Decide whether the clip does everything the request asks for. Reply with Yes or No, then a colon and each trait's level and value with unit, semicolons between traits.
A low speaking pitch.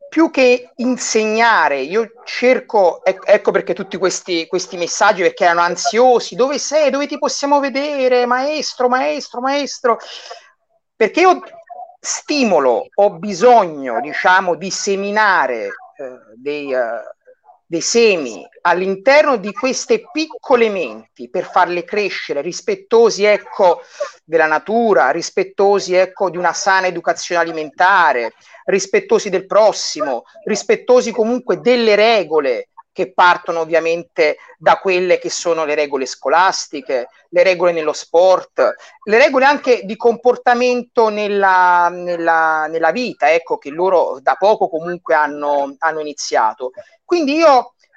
No: high, 220 Hz